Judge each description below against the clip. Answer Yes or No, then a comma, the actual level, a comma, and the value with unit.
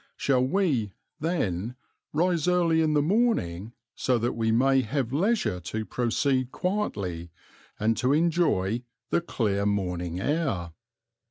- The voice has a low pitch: Yes, low, 125 Hz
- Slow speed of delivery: Yes, slow, 125 wpm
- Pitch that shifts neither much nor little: No, wide, 8.1 semitones